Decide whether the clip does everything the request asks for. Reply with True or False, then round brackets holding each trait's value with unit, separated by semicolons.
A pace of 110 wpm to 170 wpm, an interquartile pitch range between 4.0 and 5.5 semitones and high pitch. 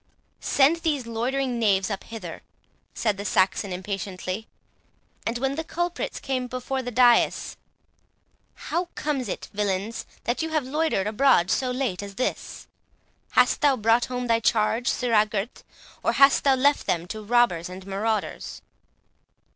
True (145 wpm; 4.8 semitones; 235 Hz)